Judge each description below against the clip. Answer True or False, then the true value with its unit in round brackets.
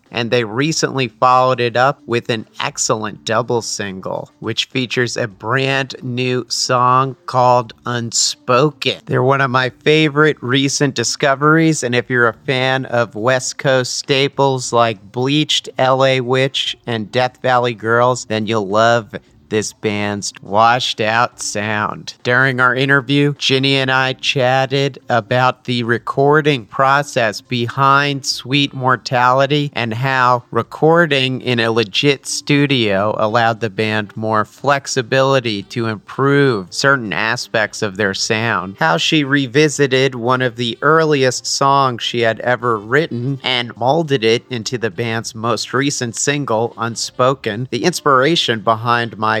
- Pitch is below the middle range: True (125 Hz)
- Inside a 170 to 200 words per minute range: False (135 wpm)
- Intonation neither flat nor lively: True (3.0 semitones)